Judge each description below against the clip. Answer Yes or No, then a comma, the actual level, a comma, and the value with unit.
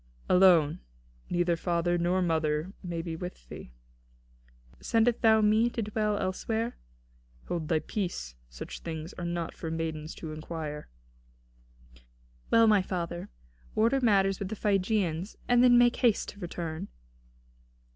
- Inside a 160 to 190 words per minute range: No, slow, 135 wpm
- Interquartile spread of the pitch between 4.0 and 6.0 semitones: Yes, average, 4.7 semitones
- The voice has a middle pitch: Yes, medium, 180 Hz